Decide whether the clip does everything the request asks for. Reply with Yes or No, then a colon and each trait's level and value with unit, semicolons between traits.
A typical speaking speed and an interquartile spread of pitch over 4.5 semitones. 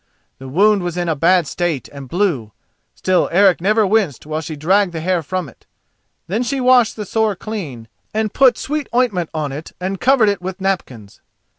Yes: average, 190 wpm; average, 5.2 semitones